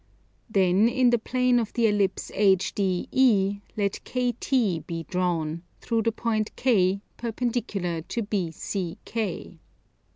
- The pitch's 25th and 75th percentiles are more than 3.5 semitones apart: Yes, average, 4.3 semitones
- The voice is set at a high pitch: Yes, high, 205 Hz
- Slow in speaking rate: Yes, slow, 110 wpm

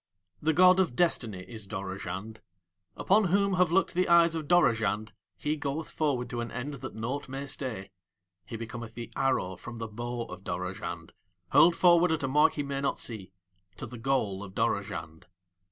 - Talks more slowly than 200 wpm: Yes, average, 180 wpm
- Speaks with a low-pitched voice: Yes, low, 125 Hz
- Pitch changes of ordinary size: No, wide, 6.5 semitones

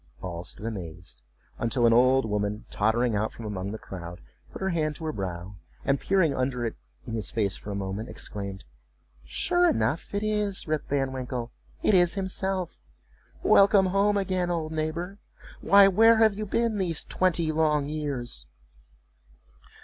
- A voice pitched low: No, medium, 145 Hz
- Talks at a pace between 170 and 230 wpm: No, average, 155 wpm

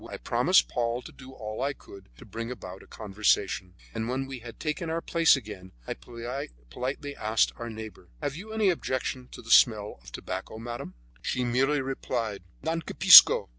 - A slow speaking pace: No, average, 180 wpm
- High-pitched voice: No, low, 120 Hz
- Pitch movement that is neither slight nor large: Yes, average, 3.9 semitones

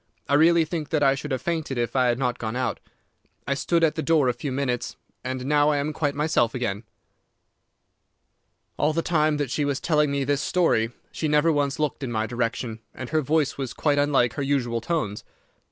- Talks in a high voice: No, medium, 140 Hz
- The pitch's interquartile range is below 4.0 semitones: Yes, average, 3.4 semitones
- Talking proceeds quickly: Yes, fast, 215 wpm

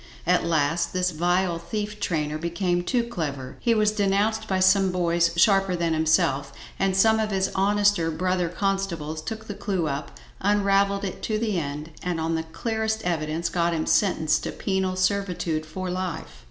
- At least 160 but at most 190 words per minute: Yes, average, 170 wpm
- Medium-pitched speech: Yes, medium, 180 Hz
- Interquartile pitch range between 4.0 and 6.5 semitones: No, average, 3.5 semitones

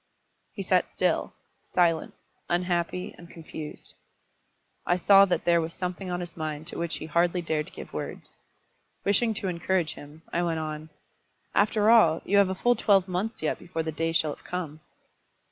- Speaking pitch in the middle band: Yes, medium, 175 Hz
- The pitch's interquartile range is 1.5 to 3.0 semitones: Yes, average, 2.7 semitones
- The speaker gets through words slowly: No, average, 180 wpm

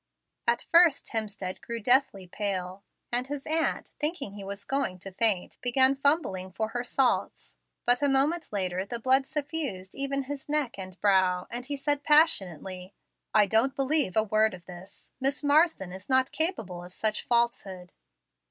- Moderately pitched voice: No, high, 235 Hz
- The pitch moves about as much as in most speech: No, wide, 6.5 semitones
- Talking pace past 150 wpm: Yes, average, 165 wpm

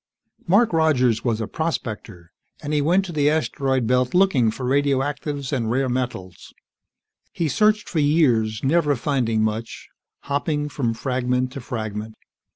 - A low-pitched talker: Yes, low, 130 Hz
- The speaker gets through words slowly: No, average, 150 wpm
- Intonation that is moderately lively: Yes, average, 4.4 semitones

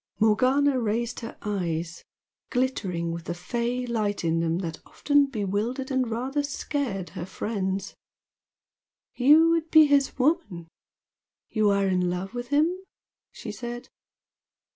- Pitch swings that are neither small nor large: No, wide, 6.1 semitones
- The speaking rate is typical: No, slow, 130 wpm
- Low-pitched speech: No, high, 230 Hz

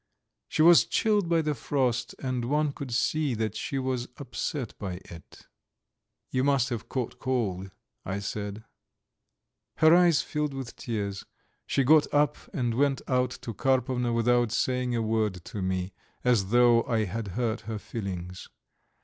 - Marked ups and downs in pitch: No, average, 4.0 semitones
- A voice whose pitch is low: Yes, low, 120 Hz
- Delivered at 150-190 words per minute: Yes, average, 155 wpm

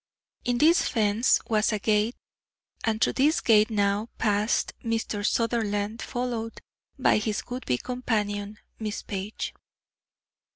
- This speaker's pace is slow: Yes, slow, 125 wpm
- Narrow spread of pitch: Yes, narrow, 2.2 semitones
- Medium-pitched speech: No, high, 220 Hz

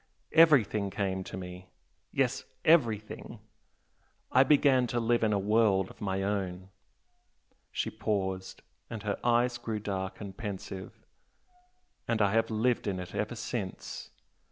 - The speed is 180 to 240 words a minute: No, average, 140 wpm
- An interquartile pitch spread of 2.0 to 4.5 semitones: Yes, average, 3.5 semitones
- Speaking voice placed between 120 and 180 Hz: No, low, 105 Hz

